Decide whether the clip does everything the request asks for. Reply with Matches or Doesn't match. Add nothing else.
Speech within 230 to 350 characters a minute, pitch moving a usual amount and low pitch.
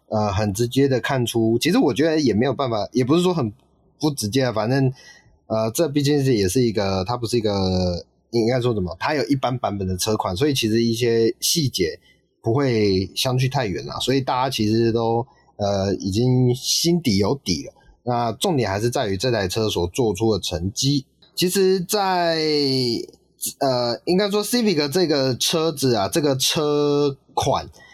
Matches